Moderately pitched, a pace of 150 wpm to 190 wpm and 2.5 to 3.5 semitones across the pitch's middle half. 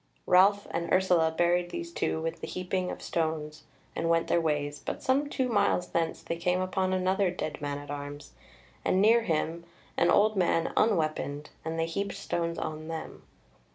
Yes: medium, 170 Hz; average, 180 wpm; average, 2.8 semitones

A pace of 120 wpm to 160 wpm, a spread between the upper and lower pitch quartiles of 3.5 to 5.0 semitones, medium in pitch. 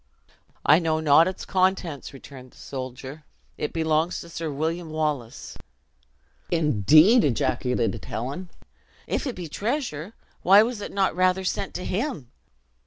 Yes: slow, 135 wpm; average, 4.7 semitones; medium, 160 Hz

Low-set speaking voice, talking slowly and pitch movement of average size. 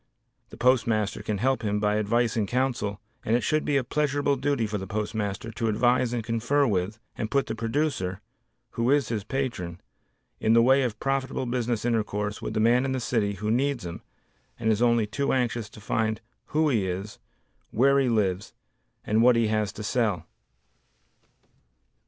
No: low, 115 Hz; average, 180 wpm; average, 3.5 semitones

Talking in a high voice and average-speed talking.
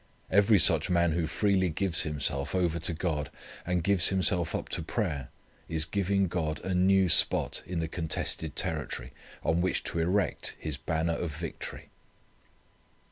No: very low, 85 Hz; average, 155 wpm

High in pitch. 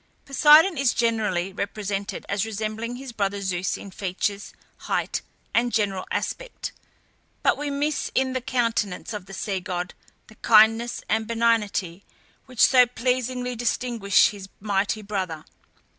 Yes: high, 220 Hz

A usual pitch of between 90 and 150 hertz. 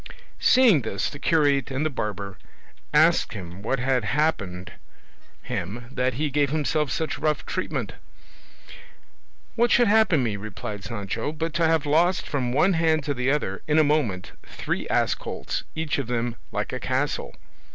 Yes: medium, 140 Hz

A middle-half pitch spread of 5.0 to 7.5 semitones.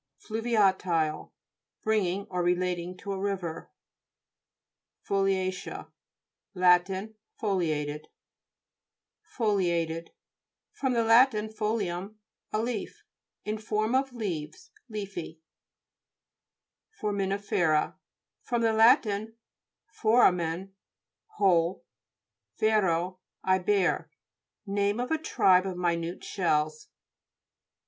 No: average, 3.7 semitones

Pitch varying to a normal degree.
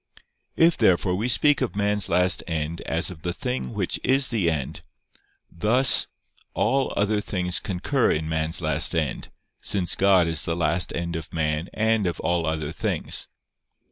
Yes: average, 4.4 semitones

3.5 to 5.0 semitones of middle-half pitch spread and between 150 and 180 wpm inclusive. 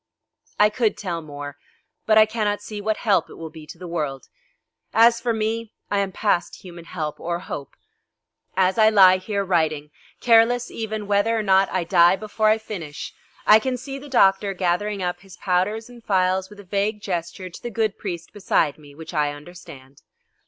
No: average, 4.0 semitones; average, 190 wpm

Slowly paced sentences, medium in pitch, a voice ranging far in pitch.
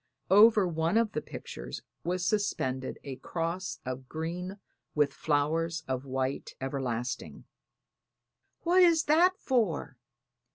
Yes: slow, 115 wpm; medium, 165 Hz; wide, 7.5 semitones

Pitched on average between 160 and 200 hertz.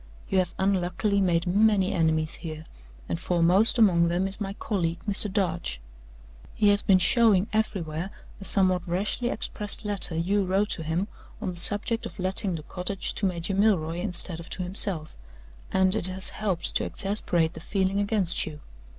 Yes: medium, 185 Hz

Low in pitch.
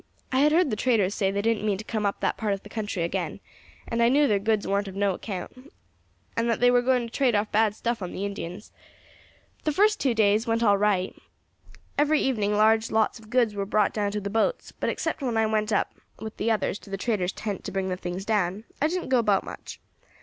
No: high, 215 Hz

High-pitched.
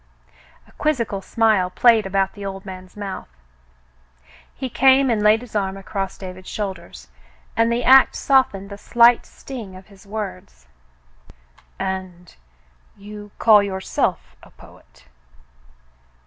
Yes: high, 200 Hz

